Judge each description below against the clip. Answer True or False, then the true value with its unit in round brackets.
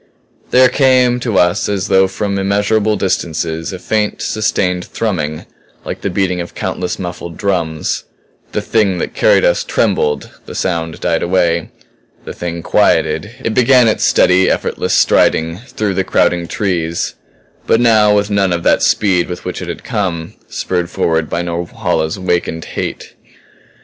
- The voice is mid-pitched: False (90 Hz)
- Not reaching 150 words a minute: False (155 wpm)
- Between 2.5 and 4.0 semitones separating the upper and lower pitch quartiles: True (3.4 semitones)